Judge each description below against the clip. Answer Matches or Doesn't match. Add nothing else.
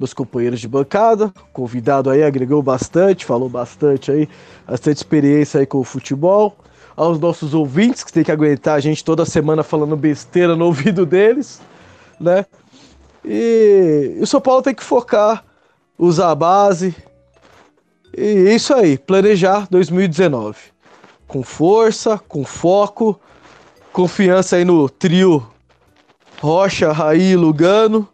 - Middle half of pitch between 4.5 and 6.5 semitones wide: Matches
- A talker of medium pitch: Matches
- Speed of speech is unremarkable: Matches